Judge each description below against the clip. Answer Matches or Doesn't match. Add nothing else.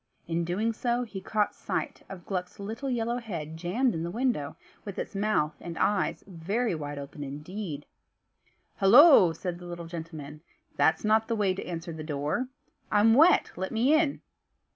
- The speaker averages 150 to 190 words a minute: Matches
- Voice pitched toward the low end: Doesn't match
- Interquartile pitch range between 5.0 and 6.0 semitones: Matches